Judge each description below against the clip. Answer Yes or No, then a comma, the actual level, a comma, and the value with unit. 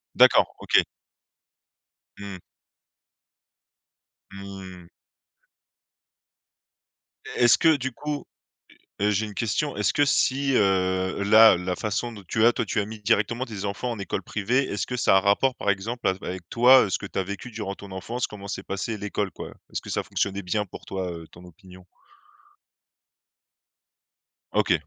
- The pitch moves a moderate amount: Yes, average, 3.5 semitones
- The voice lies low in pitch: Yes, low, 100 Hz